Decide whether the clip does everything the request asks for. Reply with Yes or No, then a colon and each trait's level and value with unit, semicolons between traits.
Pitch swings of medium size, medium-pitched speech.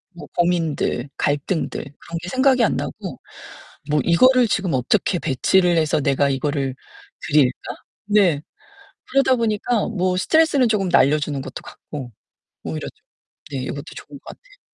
No: wide, 7.1 semitones; medium, 170 Hz